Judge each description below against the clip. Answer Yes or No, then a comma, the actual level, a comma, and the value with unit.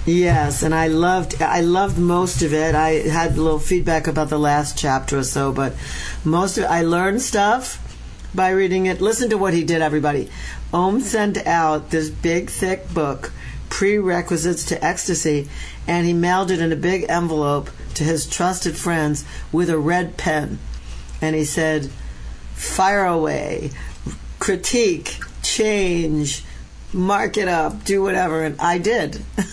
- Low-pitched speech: No, medium, 165 Hz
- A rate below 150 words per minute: No, average, 155 wpm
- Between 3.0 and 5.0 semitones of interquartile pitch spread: Yes, average, 3.5 semitones